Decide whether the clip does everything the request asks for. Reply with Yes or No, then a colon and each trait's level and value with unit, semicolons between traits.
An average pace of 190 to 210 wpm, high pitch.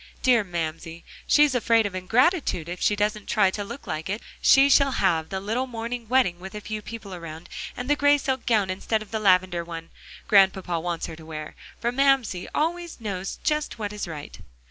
Yes: average, 195 wpm; high, 210 Hz